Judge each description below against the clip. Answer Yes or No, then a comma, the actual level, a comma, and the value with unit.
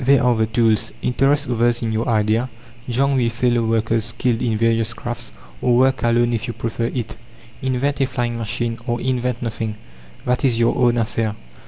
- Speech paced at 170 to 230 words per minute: Yes, average, 185 wpm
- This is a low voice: Yes, low, 120 Hz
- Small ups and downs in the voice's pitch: Yes, narrow, 1.6 semitones